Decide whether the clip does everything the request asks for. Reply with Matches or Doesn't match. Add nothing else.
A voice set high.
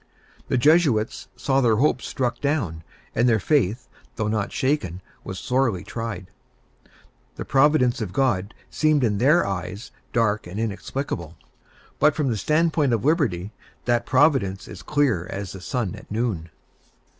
Doesn't match